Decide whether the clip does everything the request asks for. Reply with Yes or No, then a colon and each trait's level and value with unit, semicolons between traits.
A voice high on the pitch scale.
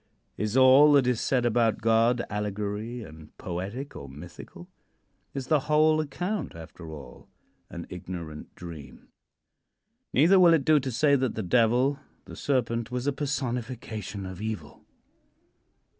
No: low, 120 Hz